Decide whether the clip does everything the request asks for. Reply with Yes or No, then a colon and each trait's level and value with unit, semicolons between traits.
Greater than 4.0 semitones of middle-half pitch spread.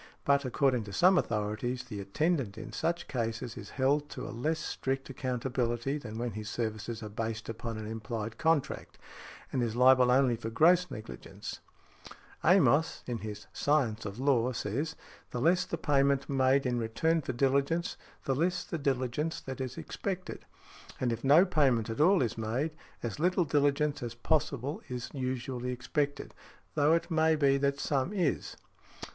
Yes: average, 4.4 semitones